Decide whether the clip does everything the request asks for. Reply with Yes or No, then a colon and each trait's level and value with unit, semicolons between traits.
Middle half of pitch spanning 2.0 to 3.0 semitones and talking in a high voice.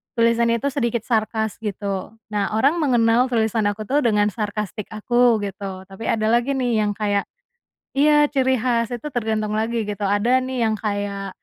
Yes: average, 2.7 semitones; high, 220 Hz